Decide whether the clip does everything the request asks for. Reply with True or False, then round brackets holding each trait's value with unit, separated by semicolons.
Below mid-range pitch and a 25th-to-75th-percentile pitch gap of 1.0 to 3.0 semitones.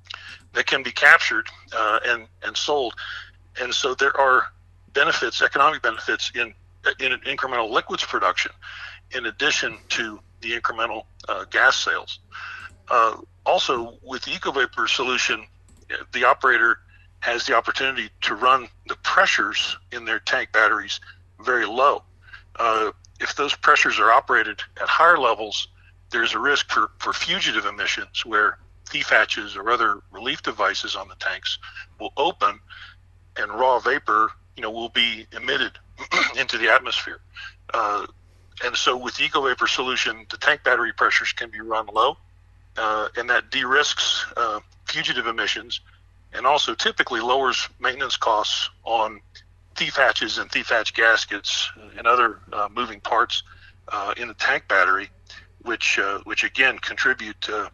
True (90 Hz; 2.6 semitones)